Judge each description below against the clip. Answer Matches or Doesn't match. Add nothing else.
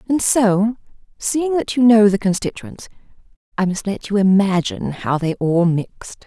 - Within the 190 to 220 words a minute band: Doesn't match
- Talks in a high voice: Matches